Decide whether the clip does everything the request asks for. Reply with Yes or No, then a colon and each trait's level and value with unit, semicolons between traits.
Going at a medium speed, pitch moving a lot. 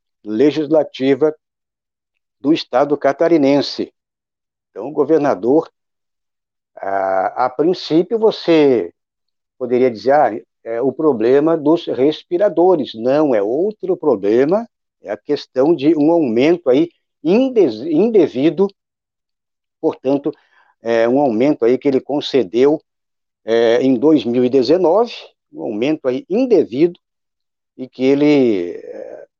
No: slow, 105 wpm; wide, 7.6 semitones